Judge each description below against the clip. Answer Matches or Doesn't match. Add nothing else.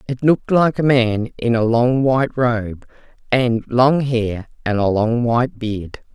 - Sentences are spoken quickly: Doesn't match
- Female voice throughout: Matches